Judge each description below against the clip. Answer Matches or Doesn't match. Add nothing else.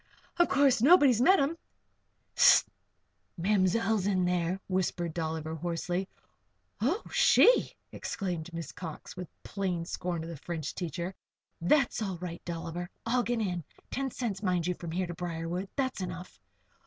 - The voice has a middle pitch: Matches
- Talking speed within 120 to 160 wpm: Matches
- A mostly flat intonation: Doesn't match